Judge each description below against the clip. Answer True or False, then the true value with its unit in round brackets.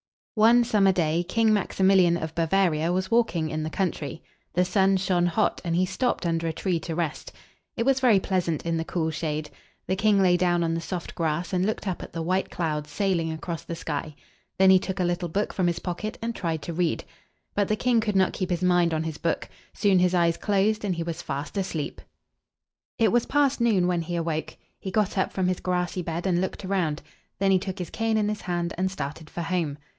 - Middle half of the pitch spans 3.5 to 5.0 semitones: False (2.8 semitones)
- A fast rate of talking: True (235 wpm)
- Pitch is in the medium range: True (180 Hz)